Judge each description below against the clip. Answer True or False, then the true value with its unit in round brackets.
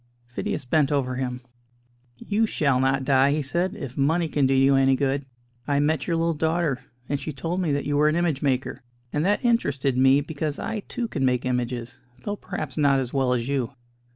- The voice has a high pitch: False (140 Hz)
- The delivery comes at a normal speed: False (210 wpm)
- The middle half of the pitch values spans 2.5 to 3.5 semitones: True (3.2 semitones)